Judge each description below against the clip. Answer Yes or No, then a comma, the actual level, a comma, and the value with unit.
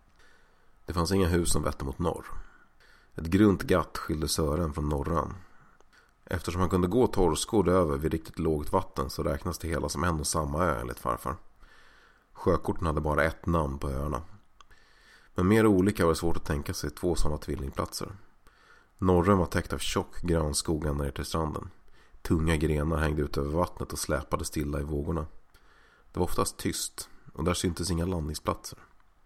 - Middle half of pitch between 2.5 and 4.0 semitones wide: Yes, average, 3.2 semitones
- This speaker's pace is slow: No, average, 175 wpm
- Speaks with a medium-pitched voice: No, very low, 80 Hz